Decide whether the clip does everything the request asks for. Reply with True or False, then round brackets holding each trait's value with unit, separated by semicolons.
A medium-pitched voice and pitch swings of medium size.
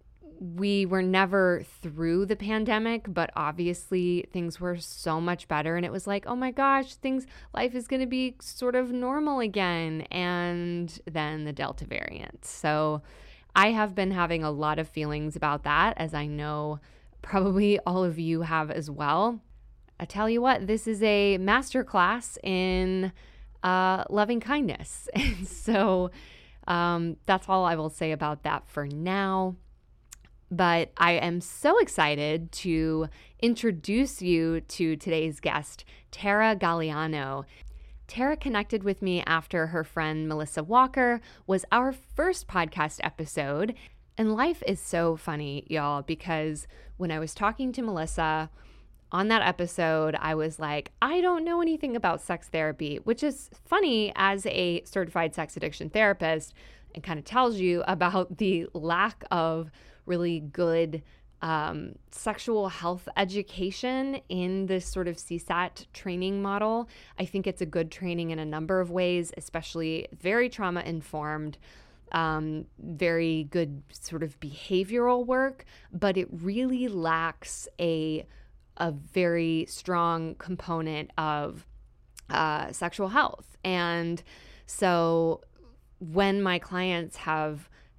True (175 Hz; 4.0 semitones)